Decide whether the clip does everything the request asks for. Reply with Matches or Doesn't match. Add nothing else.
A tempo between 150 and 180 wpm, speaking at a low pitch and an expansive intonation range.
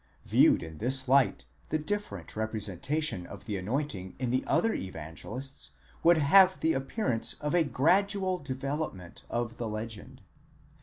Doesn't match